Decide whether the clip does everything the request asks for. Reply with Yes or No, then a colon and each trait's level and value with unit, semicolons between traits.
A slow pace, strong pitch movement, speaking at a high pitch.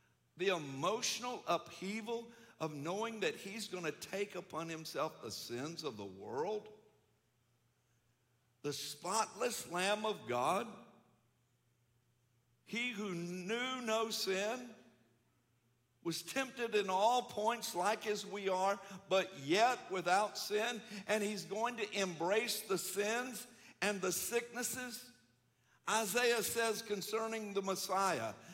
Yes: slow, 115 wpm; wide, 5.9 semitones; high, 200 Hz